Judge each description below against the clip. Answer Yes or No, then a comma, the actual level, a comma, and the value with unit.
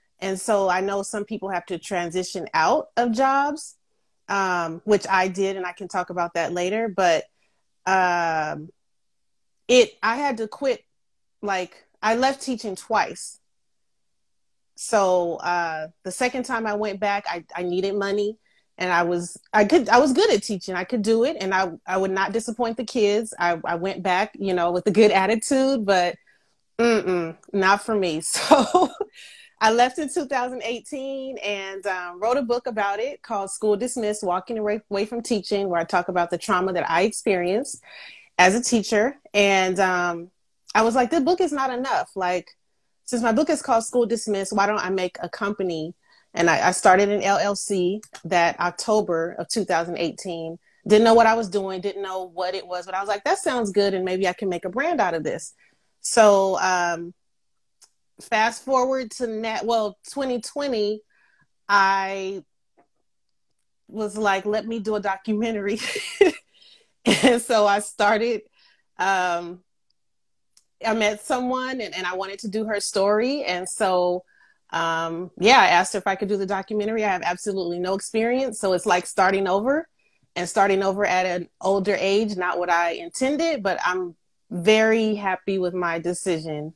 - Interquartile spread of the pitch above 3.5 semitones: Yes, average, 4.0 semitones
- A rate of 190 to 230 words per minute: No, average, 170 wpm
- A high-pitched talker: Yes, high, 200 Hz